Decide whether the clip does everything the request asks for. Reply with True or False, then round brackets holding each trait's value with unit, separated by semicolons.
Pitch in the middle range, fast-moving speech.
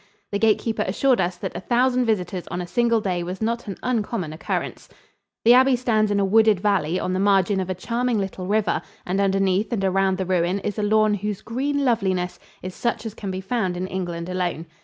False (200 Hz; 215 wpm)